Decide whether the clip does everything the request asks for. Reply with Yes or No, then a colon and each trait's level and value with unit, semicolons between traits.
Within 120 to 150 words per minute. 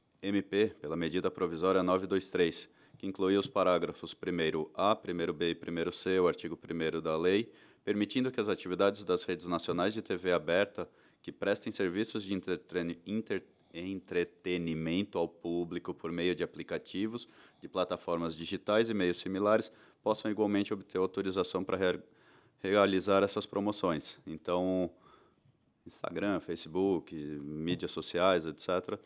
Yes: average, 125 wpm